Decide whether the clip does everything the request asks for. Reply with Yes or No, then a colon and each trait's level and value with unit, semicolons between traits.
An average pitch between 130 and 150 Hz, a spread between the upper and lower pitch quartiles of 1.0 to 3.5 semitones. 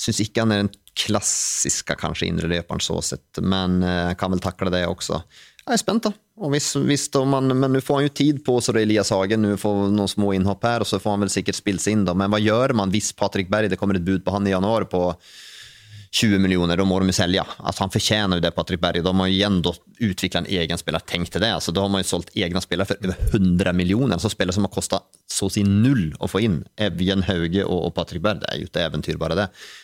No: low, 100 Hz; average, 2.8 semitones